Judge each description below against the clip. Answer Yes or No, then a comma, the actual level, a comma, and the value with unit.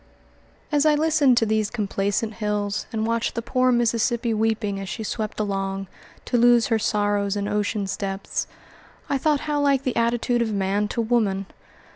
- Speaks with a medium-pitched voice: No, high, 220 Hz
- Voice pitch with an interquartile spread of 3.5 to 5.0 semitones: No, average, 2.9 semitones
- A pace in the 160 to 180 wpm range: Yes, average, 170 wpm